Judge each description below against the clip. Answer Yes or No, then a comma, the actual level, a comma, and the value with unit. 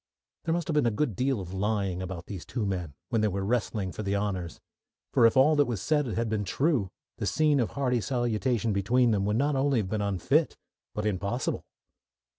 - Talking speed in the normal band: No, fast, 215 wpm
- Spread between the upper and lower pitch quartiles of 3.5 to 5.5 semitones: Yes, average, 4.6 semitones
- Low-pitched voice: Yes, low, 110 Hz